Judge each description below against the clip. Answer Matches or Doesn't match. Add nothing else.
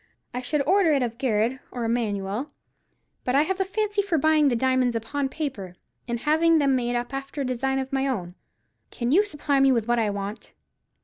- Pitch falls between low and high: Doesn't match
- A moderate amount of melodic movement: Matches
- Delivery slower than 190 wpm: Doesn't match